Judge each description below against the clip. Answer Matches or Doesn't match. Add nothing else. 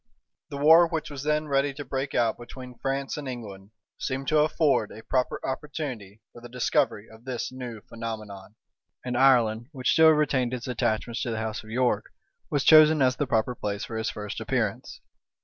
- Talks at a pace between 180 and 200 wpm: Matches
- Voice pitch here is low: Matches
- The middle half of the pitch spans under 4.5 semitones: Matches